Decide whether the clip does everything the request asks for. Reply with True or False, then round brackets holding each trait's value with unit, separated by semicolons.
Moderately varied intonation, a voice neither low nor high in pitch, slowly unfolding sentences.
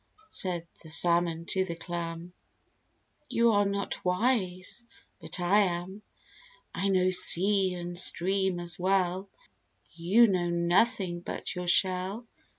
False (2.1 semitones; 180 Hz; 125 wpm)